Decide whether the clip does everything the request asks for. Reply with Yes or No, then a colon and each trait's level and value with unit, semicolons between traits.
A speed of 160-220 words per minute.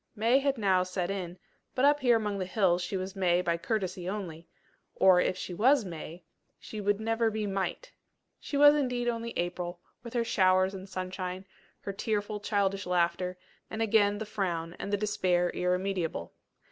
Yes: average, 175 wpm